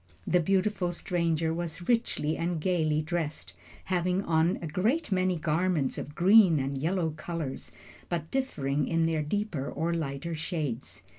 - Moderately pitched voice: Yes, medium, 165 Hz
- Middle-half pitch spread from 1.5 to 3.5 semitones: Yes, average, 3.0 semitones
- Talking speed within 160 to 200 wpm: No, average, 145 wpm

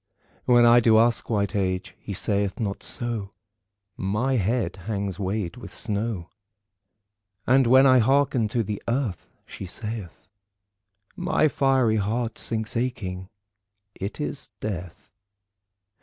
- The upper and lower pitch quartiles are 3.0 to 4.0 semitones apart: Yes, average, 3.6 semitones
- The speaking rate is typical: No, slow, 125 wpm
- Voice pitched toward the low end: Yes, low, 110 Hz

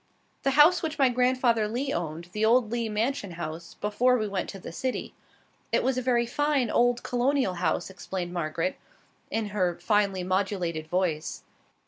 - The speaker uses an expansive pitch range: Yes, wide, 5.9 semitones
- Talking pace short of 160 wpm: No, average, 165 wpm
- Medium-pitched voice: No, high, 210 Hz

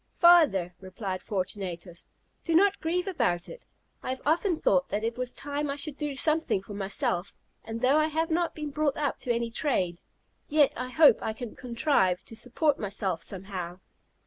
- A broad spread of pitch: Yes, wide, 7.8 semitones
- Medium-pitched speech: No, very high, 255 Hz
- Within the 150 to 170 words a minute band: No, average, 180 wpm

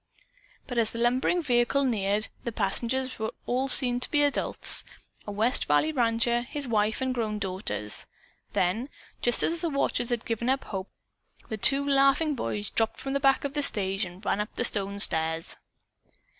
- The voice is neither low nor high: No, high, 235 Hz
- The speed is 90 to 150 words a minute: No, average, 180 wpm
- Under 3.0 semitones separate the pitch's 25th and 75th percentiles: No, average, 4.6 semitones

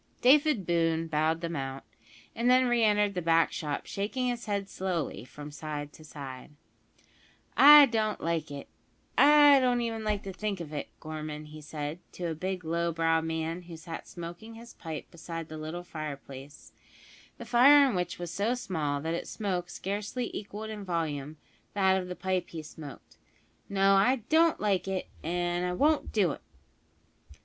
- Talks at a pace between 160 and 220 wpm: Yes, average, 175 wpm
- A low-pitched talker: No, medium, 175 Hz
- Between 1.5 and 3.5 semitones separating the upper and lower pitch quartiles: No, average, 5.1 semitones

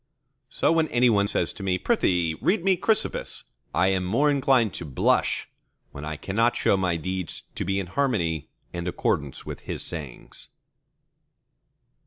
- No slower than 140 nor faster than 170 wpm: Yes, average, 160 wpm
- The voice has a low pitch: Yes, very low, 95 Hz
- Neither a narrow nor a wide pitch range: No, wide, 6.7 semitones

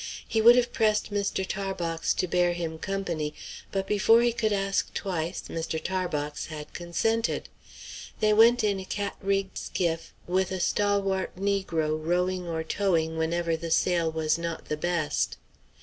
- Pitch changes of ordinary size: Yes, average, 3.4 semitones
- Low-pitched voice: No, medium, 180 Hz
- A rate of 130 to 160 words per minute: Yes, average, 155 wpm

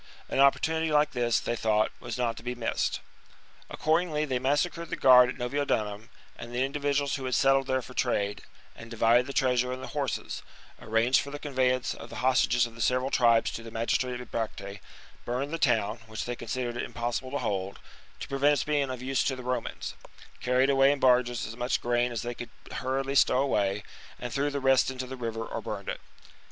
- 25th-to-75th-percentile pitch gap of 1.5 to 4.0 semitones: Yes, narrow, 2.5 semitones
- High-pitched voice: No, low, 125 Hz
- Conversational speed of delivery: No, fast, 210 wpm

